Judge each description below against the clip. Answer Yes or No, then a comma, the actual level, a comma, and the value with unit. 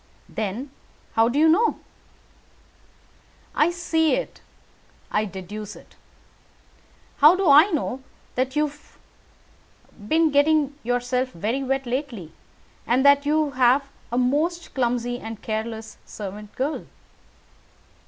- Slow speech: Yes, slow, 115 wpm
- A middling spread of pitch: Yes, average, 4.6 semitones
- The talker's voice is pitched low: No, very high, 265 Hz